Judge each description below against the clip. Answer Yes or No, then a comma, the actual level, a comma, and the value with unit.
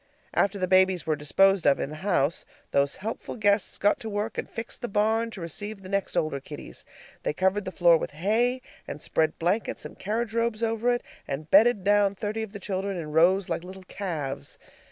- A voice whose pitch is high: Yes, high, 195 Hz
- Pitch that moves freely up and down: No, average, 4.3 semitones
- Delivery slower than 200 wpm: No, fast, 205 wpm